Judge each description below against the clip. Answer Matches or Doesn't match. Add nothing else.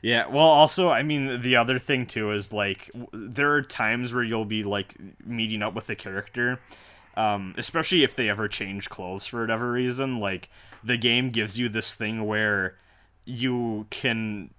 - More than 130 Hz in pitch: Doesn't match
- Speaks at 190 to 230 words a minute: Doesn't match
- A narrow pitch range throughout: Doesn't match